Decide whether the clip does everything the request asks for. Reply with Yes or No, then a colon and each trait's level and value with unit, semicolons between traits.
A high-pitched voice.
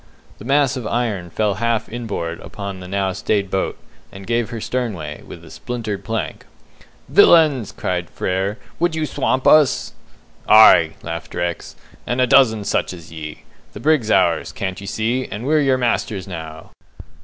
No: low, 105 Hz